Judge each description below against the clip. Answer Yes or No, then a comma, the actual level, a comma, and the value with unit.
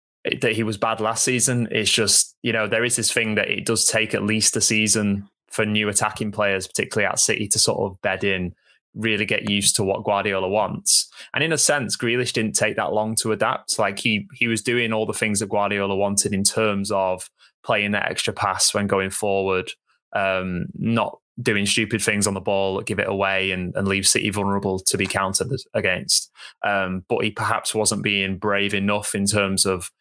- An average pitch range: No, narrow, 1.9 semitones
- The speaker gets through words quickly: Yes, fast, 210 wpm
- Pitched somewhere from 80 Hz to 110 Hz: Yes, low, 100 Hz